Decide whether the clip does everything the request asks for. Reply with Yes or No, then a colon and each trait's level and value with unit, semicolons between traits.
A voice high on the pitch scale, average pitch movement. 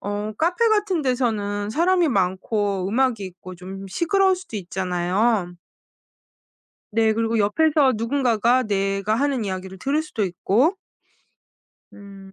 No: high, 215 Hz; wide, 5.9 semitones